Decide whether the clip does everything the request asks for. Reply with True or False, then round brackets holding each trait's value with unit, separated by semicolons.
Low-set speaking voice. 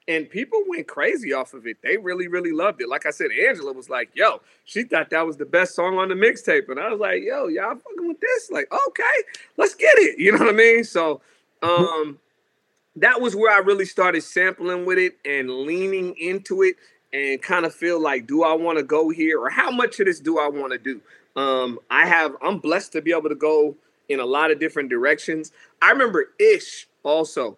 False (180 Hz)